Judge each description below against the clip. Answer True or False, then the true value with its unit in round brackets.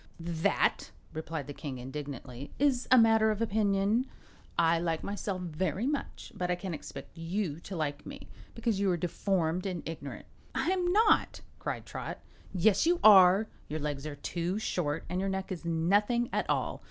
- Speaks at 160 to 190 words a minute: True (165 wpm)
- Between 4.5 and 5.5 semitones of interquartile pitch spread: True (5.1 semitones)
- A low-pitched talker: False (180 Hz)